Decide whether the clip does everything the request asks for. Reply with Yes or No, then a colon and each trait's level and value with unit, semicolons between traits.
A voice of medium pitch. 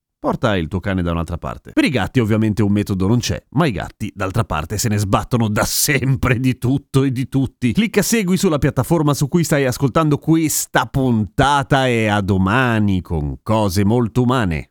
No: low, 120 Hz